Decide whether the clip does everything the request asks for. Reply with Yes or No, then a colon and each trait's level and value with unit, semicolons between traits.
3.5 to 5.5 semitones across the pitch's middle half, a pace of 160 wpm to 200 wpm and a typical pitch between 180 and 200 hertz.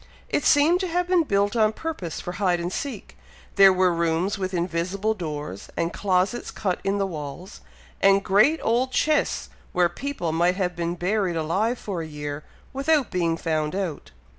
Yes: average, 4.4 semitones; average, 175 wpm; high, 190 Hz